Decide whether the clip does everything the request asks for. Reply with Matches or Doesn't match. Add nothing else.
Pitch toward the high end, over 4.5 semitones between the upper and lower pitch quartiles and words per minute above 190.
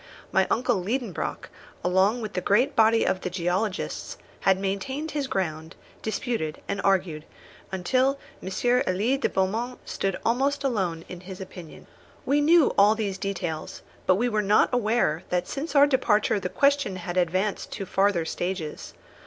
Doesn't match